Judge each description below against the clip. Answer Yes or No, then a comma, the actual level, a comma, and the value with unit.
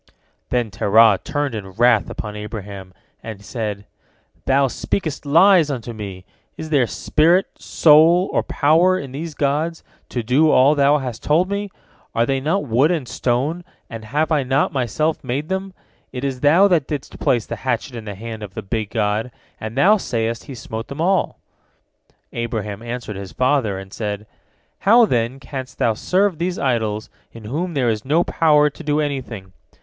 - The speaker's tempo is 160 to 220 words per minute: Yes, average, 175 wpm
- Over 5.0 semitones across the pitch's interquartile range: Yes, wide, 5.6 semitones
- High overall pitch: No, low, 130 Hz